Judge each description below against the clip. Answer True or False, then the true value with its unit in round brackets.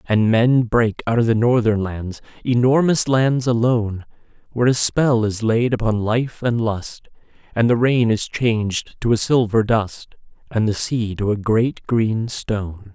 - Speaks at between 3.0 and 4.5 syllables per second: True (4.3 syllables/s)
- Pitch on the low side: True (115 Hz)